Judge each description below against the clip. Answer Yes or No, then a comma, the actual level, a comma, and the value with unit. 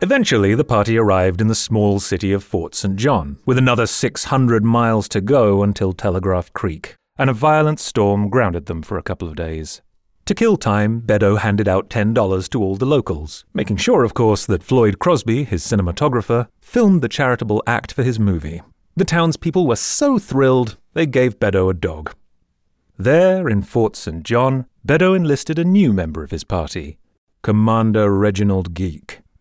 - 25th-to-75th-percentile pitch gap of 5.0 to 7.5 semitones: Yes, average, 5.3 semitones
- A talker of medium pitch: No, low, 105 Hz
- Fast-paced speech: No, average, 175 wpm